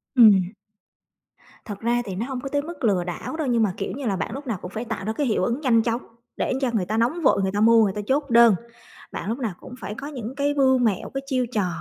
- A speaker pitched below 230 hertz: No, high, 235 Hz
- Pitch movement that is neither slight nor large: Yes, average, 4.3 semitones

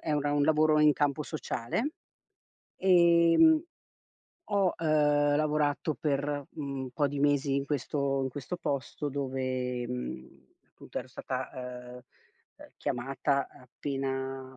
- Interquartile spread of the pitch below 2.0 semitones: No, narrow, 2.4 semitones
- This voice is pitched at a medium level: Yes, medium, 145 Hz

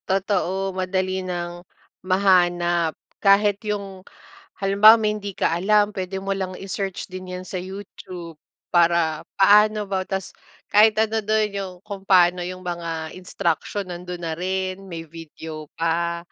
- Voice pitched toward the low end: No, medium, 185 Hz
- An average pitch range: No, narrow, 2.3 semitones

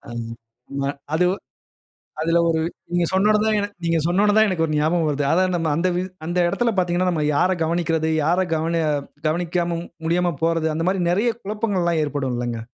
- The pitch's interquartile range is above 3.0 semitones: No, narrow, 2.4 semitones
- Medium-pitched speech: Yes, medium, 170 Hz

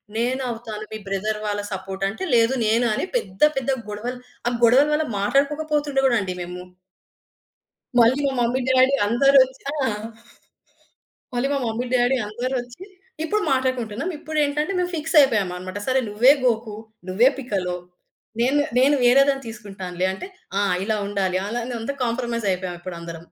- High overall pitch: Yes, high, 240 Hz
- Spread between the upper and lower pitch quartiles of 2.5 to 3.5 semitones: No, average, 4.7 semitones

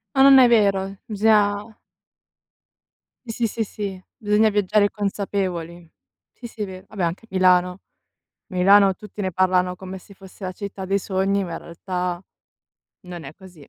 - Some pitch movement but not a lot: No, narrow, 2.2 semitones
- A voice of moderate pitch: No, high, 195 Hz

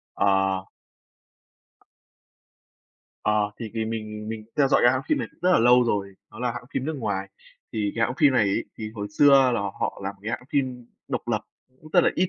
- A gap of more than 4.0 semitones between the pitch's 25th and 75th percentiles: No, average, 3.7 semitones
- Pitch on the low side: Yes, low, 110 Hz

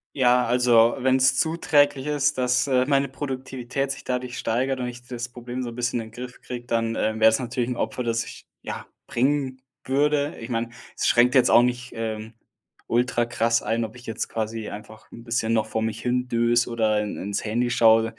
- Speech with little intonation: Yes, narrow, 2.1 semitones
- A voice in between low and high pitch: No, low, 120 Hz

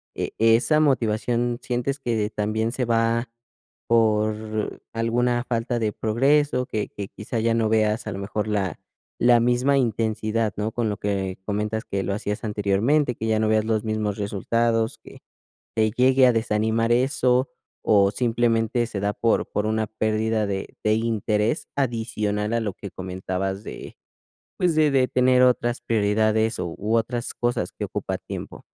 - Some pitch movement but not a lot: No, narrow, 2.3 semitones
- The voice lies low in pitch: Yes, low, 110 Hz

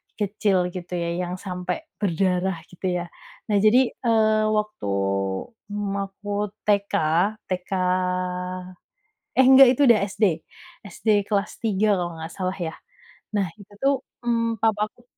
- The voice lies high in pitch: Yes, high, 200 Hz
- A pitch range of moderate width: Yes, average, 3.1 semitones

